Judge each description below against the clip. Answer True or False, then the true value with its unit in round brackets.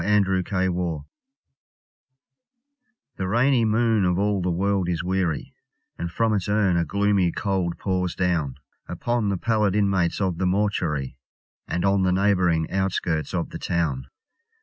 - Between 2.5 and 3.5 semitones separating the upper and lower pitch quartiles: True (2.8 semitones)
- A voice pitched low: True (95 Hz)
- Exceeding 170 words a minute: False (140 wpm)